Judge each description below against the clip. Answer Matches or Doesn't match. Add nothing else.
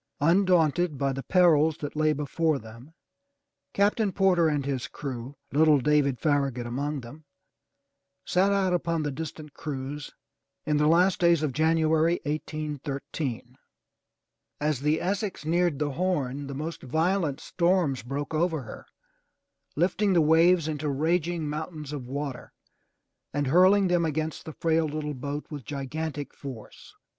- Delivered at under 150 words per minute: Matches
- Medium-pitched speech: Matches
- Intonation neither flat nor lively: Matches